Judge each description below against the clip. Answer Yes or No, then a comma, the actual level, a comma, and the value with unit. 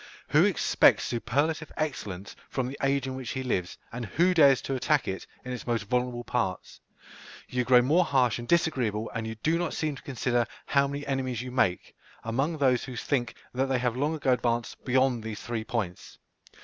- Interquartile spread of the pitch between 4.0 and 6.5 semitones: No, average, 2.9 semitones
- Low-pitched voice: Yes, low, 125 Hz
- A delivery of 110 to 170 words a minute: No, average, 195 wpm